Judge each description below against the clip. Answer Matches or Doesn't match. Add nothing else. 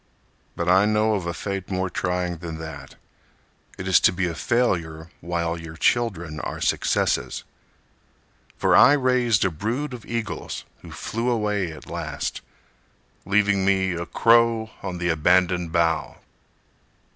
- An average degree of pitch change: Matches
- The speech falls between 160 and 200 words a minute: Doesn't match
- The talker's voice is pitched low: Matches